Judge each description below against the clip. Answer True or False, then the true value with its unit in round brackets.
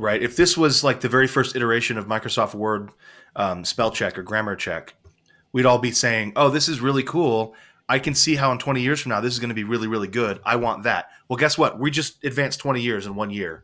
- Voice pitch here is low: True (125 Hz)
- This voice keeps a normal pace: False (255 wpm)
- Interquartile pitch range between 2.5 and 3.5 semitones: False (3.9 semitones)